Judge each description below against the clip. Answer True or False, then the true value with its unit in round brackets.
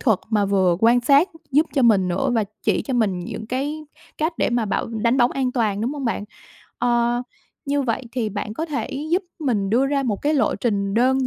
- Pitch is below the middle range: False (240 Hz)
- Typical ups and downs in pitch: True (4.2 semitones)